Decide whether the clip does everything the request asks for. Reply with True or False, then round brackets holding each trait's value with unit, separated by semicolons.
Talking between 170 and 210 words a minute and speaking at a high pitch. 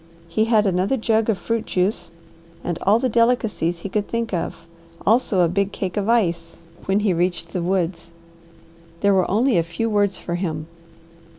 True (180 wpm; 195 Hz)